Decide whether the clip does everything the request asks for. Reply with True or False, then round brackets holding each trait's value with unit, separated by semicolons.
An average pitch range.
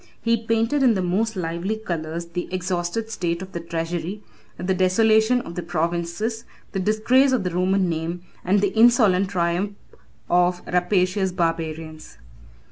True (4.1 semitones)